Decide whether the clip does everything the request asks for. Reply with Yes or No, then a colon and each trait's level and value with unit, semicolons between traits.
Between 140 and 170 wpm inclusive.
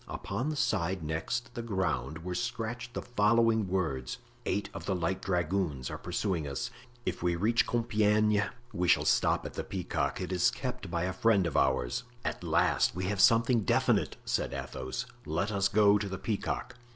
No: average, 180 wpm